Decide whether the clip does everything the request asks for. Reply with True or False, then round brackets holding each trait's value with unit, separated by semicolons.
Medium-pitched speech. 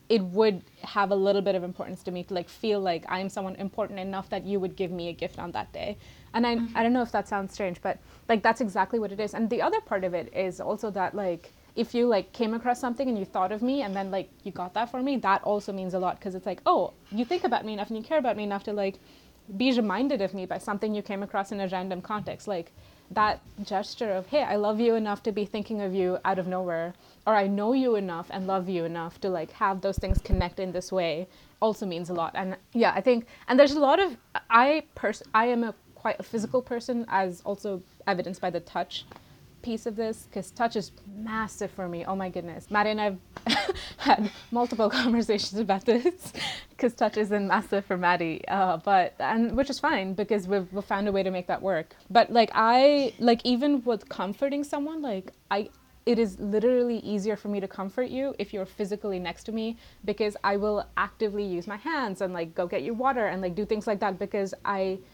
False (205 Hz)